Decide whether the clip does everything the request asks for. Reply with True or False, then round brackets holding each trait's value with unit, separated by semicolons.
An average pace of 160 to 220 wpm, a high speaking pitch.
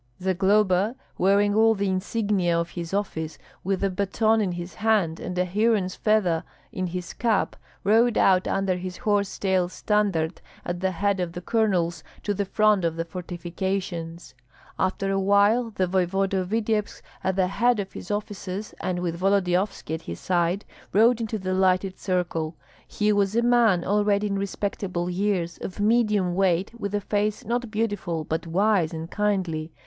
True (170 wpm; 195 Hz)